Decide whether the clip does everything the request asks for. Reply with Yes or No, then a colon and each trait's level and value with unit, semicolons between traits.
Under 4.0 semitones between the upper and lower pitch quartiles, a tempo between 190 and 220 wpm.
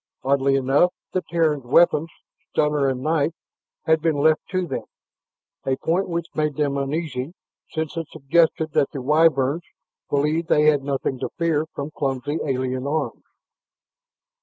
No: average, 2.8 semitones; average, 145 wpm